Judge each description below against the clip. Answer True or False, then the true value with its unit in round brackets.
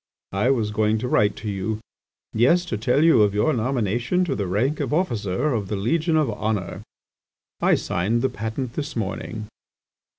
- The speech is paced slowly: False (175 wpm)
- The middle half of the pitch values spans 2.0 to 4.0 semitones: False (4.6 semitones)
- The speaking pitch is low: True (115 Hz)